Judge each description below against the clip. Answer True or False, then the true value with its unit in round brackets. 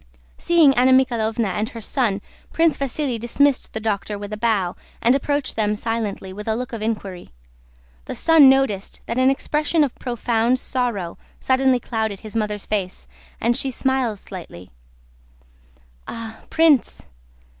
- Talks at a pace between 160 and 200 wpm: False (150 wpm)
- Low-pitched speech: False (230 Hz)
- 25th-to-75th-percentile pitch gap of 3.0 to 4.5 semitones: True (3.9 semitones)